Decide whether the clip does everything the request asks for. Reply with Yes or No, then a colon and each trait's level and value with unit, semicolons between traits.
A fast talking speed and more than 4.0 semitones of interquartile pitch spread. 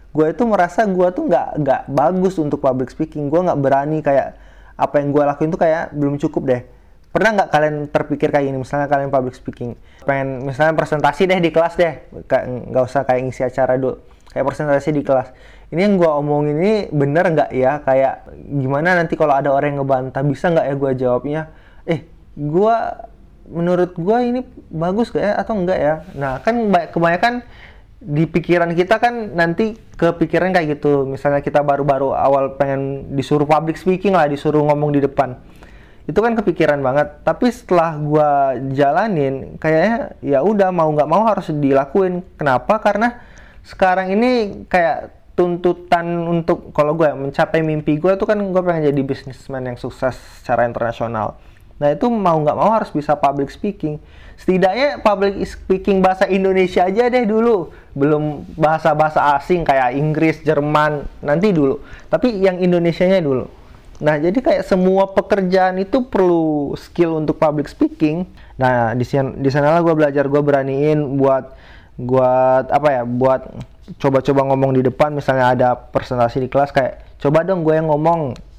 Yes: fast, 165 wpm; average, 4.7 semitones